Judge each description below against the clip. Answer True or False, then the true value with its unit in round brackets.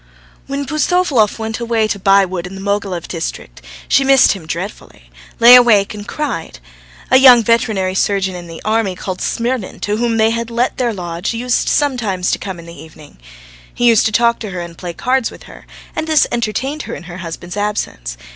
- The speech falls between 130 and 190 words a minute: False (205 wpm)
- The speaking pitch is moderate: False (210 Hz)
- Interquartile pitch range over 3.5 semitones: True (4.6 semitones)